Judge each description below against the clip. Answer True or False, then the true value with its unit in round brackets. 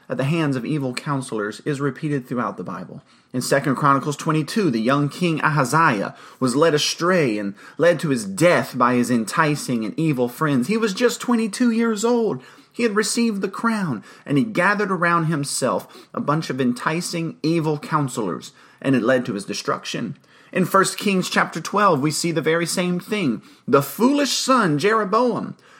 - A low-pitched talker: False (165 Hz)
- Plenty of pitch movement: True (6.8 semitones)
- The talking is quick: False (180 wpm)